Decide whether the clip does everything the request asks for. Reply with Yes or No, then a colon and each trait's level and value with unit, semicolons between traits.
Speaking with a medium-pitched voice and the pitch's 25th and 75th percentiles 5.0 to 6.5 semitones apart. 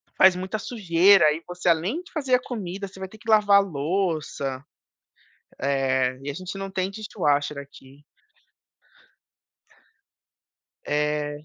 Yes: medium, 180 Hz; average, 5.3 semitones